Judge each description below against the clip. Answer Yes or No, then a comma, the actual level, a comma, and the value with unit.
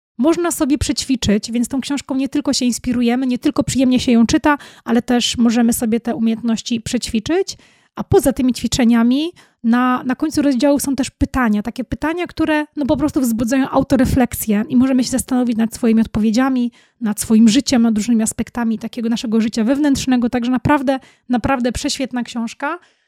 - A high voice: Yes, very high, 250 Hz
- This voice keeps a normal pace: No, fast, 165 wpm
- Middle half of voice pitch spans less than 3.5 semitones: Yes, average, 3.0 semitones